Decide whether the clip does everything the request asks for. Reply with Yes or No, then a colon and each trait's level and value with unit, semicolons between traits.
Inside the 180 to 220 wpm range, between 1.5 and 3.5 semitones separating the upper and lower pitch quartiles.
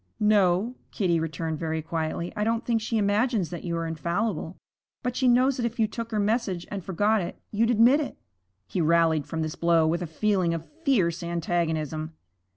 No: average, 190 wpm; average, 5.1 semitones